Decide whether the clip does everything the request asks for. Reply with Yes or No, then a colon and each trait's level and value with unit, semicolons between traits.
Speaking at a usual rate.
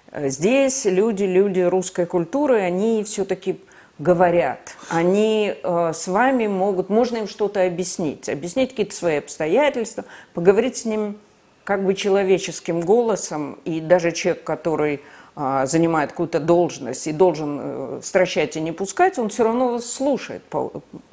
Yes: average, 140 wpm